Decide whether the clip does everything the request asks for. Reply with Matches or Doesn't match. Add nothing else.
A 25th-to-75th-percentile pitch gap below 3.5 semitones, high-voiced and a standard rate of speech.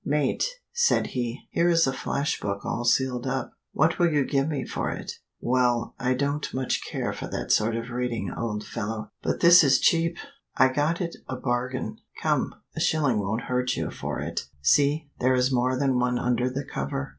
Doesn't match